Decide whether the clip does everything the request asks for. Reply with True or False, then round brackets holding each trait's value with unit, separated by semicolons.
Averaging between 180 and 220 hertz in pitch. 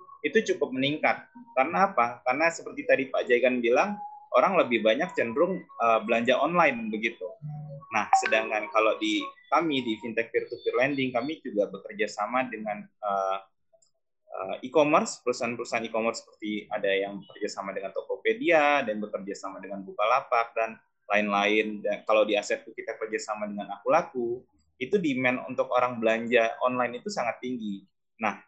False (120 Hz)